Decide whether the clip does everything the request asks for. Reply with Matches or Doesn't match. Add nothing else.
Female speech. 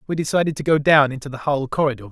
Doesn't match